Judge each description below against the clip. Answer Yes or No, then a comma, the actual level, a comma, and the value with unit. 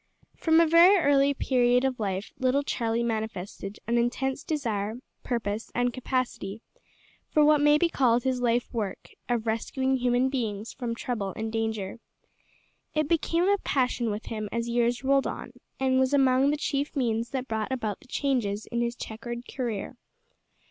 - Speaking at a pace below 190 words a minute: Yes, average, 165 wpm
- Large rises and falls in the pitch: No, average, 3.2 semitones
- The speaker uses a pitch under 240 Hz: No, high, 245 Hz